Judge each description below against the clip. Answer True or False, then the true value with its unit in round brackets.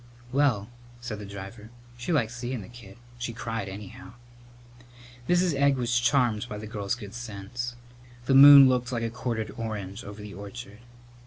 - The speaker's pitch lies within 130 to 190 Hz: False (115 Hz)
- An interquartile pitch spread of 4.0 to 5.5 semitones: False (3.0 semitones)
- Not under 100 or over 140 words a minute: False (165 wpm)